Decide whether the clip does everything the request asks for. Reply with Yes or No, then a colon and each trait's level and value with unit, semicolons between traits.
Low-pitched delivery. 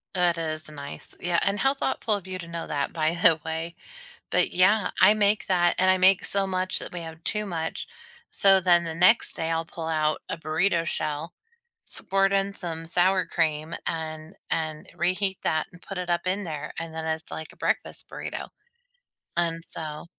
No: medium, 170 Hz